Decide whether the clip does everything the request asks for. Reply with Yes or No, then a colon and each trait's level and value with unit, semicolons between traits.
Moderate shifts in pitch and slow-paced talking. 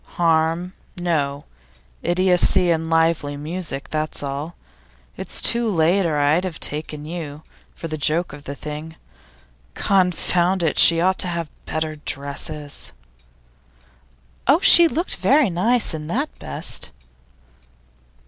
Yes: average, 3.1 semitones; slow, 125 wpm